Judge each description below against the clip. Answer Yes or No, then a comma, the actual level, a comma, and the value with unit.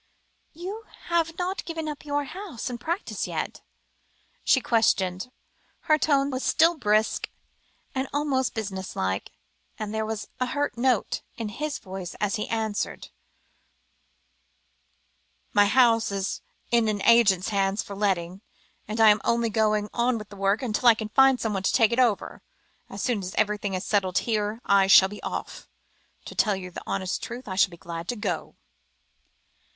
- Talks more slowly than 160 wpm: No, average, 165 wpm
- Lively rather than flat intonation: No, average, 4.4 semitones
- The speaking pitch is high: Yes, high, 220 Hz